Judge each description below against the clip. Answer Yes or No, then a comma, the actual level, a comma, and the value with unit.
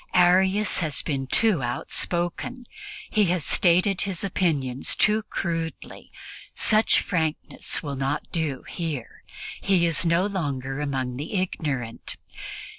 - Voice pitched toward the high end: No, medium, 165 Hz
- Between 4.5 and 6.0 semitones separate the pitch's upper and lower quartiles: Yes, average, 5.2 semitones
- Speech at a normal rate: No, slow, 115 wpm